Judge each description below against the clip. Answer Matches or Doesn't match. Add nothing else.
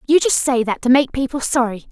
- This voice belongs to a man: Doesn't match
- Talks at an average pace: Doesn't match